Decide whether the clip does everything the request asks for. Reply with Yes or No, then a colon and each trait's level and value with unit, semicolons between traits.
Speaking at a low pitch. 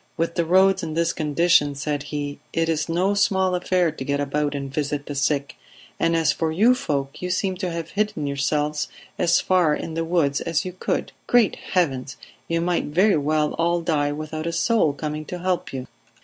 No: medium, 160 Hz